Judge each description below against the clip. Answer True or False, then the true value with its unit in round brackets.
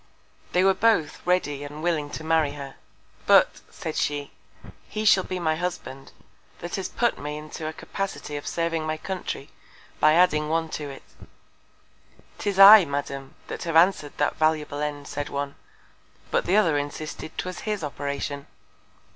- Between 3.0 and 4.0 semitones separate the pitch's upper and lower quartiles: True (3.7 semitones)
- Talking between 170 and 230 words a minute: False (160 wpm)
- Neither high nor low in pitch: True (155 Hz)